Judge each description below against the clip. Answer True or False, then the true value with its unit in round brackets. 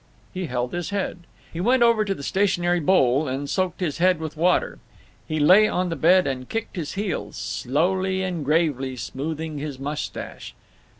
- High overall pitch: False (170 Hz)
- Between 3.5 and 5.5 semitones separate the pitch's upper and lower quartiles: True (4.4 semitones)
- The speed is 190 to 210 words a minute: False (175 wpm)